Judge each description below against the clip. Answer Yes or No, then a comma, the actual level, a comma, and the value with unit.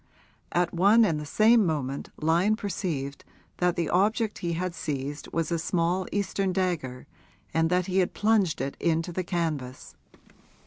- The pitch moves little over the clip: No, average, 3.5 semitones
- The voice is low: No, medium, 175 Hz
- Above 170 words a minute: No, average, 155 wpm